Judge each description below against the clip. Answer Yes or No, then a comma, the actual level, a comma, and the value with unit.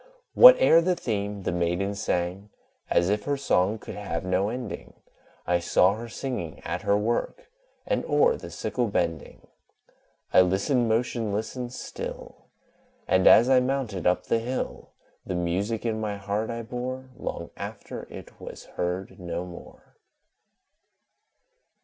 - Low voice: Yes, low, 105 Hz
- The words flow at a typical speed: Yes, average, 145 wpm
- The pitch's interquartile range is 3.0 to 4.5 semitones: No, average, 5.0 semitones